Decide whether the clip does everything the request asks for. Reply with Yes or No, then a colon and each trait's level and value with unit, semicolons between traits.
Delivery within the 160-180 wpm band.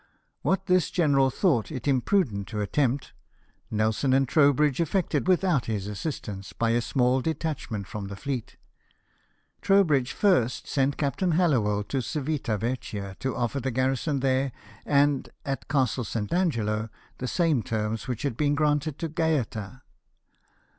No: average, 140 wpm